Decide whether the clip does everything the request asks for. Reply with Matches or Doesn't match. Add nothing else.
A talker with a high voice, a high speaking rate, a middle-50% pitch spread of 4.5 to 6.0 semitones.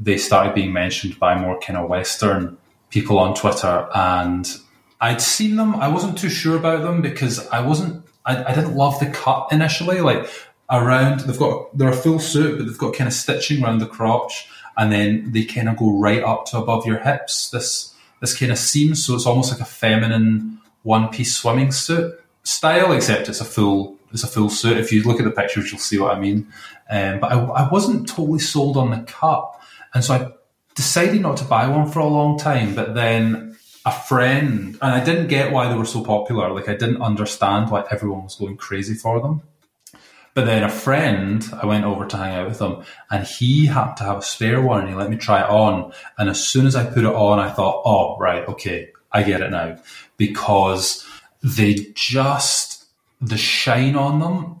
Doesn't match